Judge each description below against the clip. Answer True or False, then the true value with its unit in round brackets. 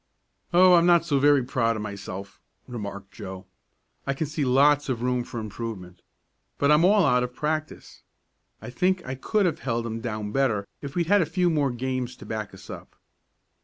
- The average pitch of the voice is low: True (130 Hz)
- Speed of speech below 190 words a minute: False (195 wpm)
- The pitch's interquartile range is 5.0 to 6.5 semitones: True (5.5 semitones)